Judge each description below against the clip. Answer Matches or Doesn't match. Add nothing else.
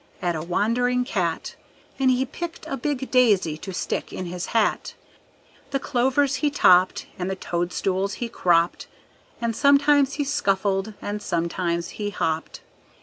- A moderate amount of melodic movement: Doesn't match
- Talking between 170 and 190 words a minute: Doesn't match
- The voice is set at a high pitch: Matches